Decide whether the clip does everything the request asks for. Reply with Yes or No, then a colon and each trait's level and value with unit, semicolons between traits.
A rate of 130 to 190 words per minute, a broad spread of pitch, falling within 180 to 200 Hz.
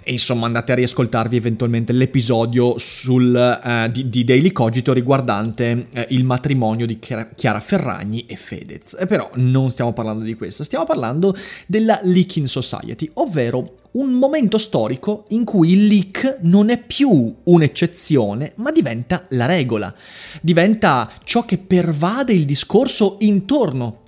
No: average, 140 wpm; wide, 8.0 semitones; low, 135 Hz